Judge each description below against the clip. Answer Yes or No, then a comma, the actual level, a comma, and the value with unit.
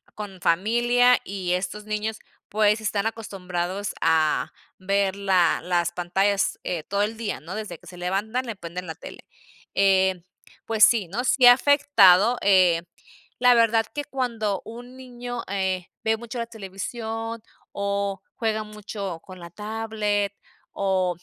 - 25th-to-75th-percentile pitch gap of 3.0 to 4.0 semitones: Yes, average, 3.3 semitones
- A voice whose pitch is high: Yes, high, 205 Hz